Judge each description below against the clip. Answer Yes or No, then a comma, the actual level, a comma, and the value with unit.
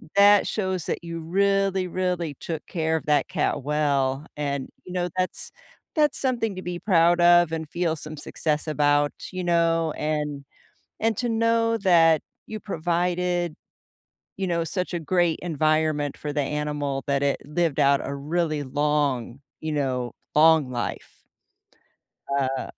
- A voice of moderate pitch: Yes, medium, 160 Hz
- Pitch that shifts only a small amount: No, average, 3.5 semitones